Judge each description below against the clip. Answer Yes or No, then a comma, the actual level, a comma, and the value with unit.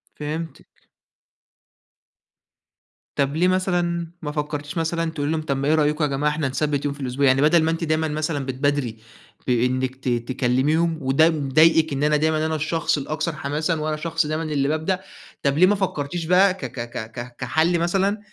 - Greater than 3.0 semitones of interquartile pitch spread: No, average, 2.7 semitones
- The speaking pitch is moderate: Yes, medium, 155 Hz